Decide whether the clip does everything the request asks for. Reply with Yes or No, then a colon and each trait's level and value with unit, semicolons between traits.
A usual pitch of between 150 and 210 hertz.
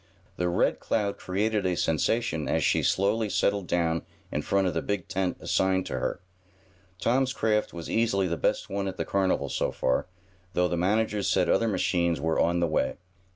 No: very low, 95 Hz